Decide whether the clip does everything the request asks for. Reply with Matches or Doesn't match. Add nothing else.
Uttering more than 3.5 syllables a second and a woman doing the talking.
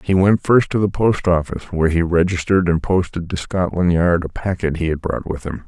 Doesn't match